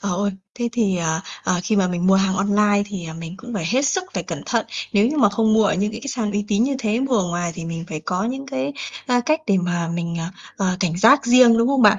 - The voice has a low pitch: No, high, 205 Hz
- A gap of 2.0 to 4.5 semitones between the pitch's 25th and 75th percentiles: No, average, 5.0 semitones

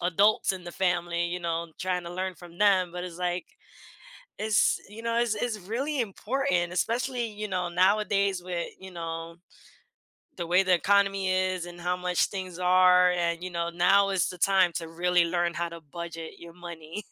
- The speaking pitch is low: No, medium, 180 Hz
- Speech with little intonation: Yes, narrow, 2.3 semitones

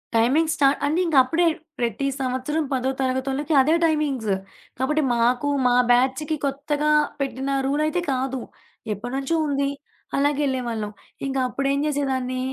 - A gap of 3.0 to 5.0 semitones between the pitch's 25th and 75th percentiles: No, narrow, 2.5 semitones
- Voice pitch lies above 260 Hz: Yes, very high, 275 Hz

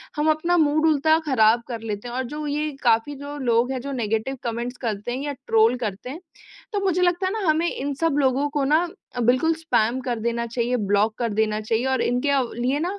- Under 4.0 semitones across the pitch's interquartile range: No, average, 4.3 semitones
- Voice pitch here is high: Yes, very high, 260 Hz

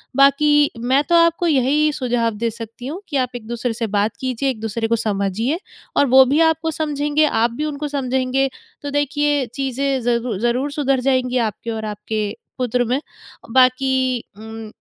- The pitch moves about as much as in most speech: Yes, average, 3.6 semitones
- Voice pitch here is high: Yes, very high, 255 Hz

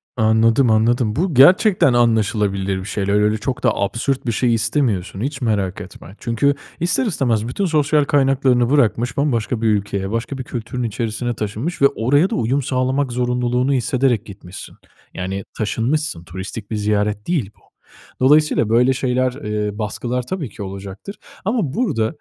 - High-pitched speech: No, low, 120 Hz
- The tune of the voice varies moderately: Yes, average, 4.4 semitones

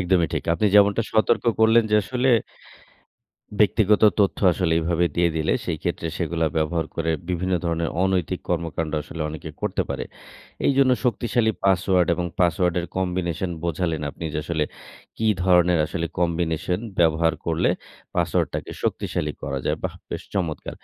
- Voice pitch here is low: Yes, very low, 85 Hz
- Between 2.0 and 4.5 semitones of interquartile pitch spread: Yes, narrow, 2.6 semitones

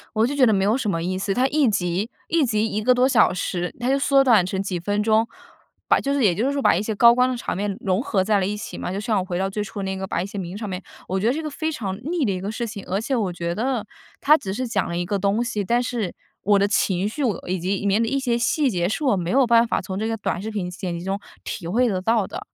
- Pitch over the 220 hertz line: No, high, 210 Hz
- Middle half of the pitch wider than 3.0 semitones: Yes, average, 4.1 semitones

